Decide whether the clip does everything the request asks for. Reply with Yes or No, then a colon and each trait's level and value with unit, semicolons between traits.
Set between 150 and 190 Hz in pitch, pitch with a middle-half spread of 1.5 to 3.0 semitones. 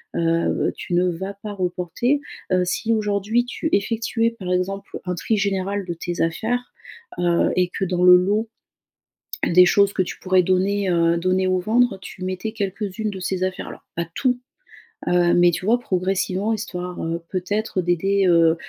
Yes: medium, 185 Hz; narrow, 2.6 semitones